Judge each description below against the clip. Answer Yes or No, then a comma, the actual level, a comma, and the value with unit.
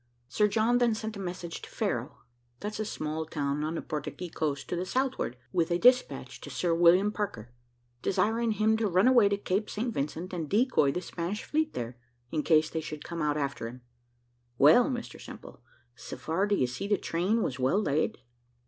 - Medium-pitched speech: Yes, medium, 180 Hz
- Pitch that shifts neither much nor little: No, wide, 5.9 semitones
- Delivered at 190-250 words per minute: Yes, average, 195 wpm